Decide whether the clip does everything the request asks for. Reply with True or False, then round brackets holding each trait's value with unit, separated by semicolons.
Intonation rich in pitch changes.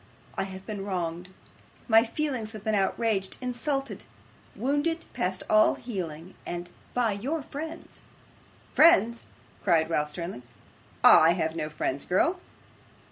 True (6.3 semitones)